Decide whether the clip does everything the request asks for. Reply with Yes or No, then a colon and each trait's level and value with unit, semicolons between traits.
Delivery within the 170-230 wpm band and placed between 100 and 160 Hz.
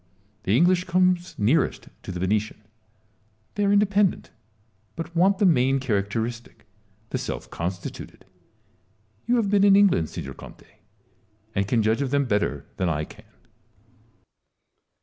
No: slow, 135 wpm; low, 135 Hz